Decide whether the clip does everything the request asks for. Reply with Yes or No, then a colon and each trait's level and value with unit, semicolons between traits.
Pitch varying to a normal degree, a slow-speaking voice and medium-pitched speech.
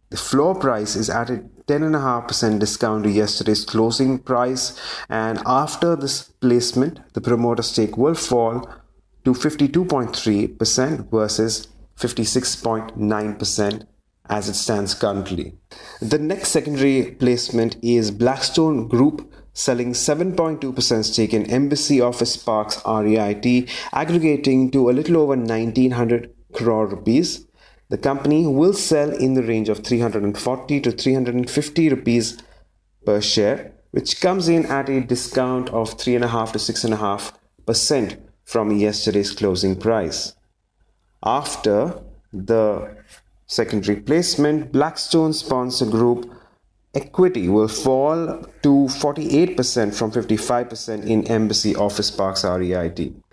No: average, 3.9 semitones; slow, 110 wpm; low, 120 Hz